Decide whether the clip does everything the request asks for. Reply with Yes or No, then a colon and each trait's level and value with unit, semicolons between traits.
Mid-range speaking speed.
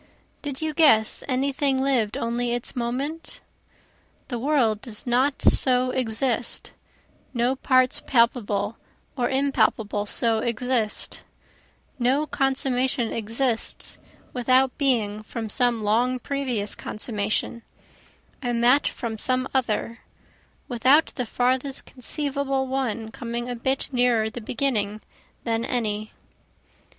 No: slow, 110 wpm